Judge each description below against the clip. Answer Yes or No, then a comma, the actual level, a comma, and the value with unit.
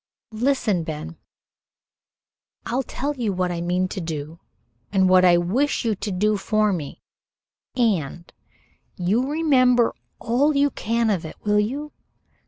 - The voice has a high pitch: Yes, high, 210 Hz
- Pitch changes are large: Yes, wide, 5.9 semitones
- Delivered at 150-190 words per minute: No, average, 140 wpm